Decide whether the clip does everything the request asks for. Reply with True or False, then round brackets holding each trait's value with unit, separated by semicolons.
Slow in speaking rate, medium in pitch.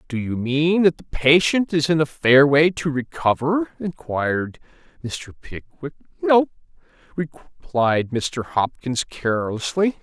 True (125 wpm; 145 Hz)